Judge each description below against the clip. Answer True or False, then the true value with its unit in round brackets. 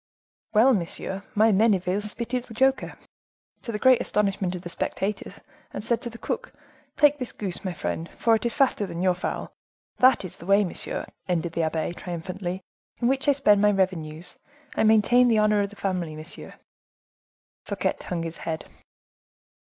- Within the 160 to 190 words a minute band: True (175 wpm)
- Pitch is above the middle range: True (200 Hz)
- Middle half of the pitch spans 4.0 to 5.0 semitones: True (4.6 semitones)